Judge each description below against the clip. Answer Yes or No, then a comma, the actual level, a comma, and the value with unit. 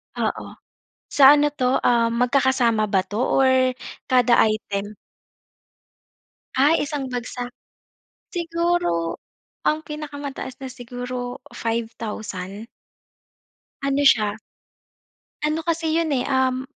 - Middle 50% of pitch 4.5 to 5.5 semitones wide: No, average, 3.8 semitones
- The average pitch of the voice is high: Yes, very high, 255 Hz